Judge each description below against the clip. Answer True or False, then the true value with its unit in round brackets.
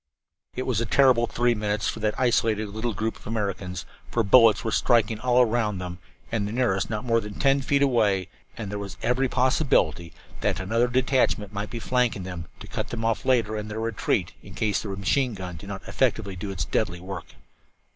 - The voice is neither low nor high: False (110 Hz)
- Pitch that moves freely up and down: False (3.6 semitones)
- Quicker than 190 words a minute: True (200 wpm)